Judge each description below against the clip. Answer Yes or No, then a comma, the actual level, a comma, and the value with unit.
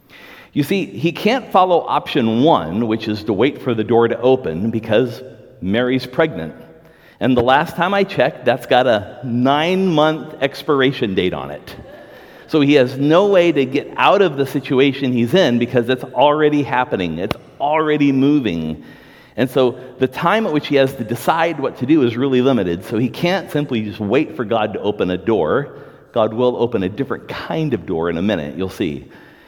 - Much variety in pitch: No, average, 4.0 semitones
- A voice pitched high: No, low, 135 Hz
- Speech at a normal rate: Yes, average, 195 wpm